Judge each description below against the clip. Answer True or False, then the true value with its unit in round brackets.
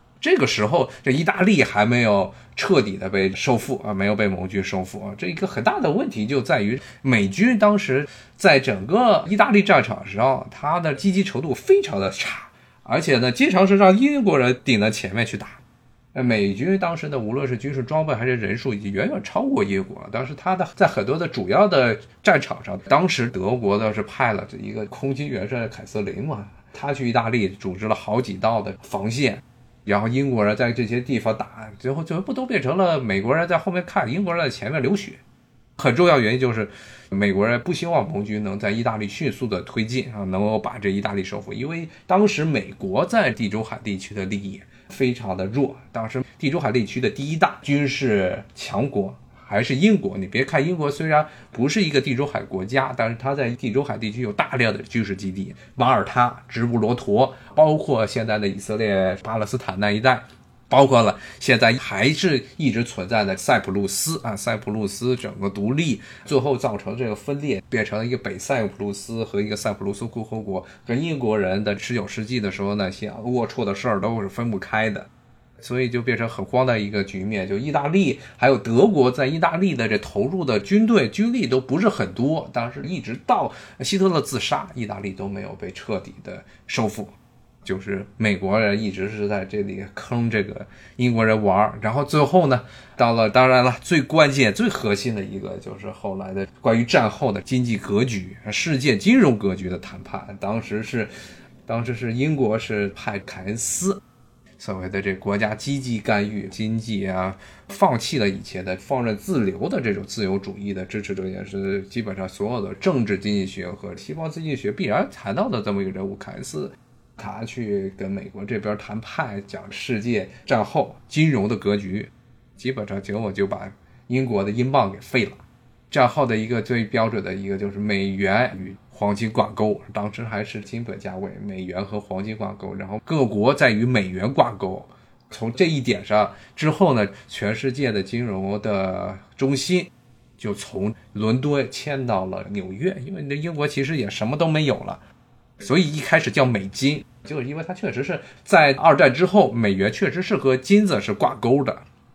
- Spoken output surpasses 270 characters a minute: True (290 characters per minute)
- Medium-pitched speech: False (115 Hz)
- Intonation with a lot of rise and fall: False (4.9 semitones)